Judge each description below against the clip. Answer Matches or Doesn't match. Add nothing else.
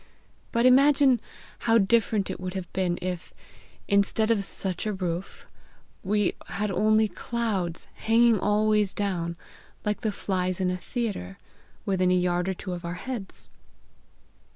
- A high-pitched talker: Matches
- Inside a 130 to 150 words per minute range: Matches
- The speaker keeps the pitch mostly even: Doesn't match